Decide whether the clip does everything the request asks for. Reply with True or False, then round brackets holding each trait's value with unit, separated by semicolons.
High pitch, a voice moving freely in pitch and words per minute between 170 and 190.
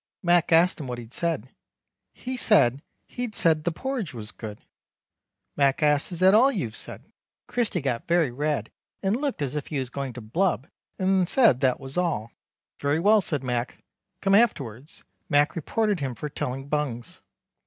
False (150 Hz; 6.6 semitones; 175 wpm)